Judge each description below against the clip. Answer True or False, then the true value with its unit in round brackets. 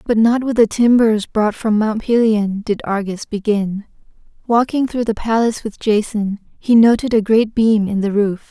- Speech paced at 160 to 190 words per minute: True (185 wpm)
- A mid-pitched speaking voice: False (215 Hz)